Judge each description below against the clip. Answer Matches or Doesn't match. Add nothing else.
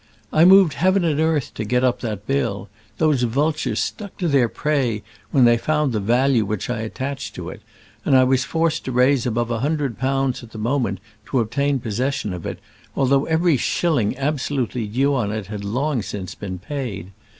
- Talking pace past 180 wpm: Matches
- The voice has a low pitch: Matches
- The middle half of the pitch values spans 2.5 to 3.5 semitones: Doesn't match